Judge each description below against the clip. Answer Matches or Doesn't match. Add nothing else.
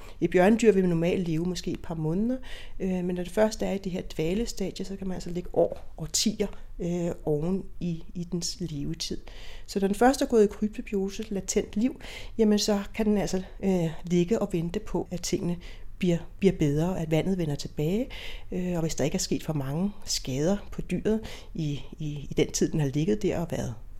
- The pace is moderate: Matches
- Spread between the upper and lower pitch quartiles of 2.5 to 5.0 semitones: Matches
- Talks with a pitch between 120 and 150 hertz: Doesn't match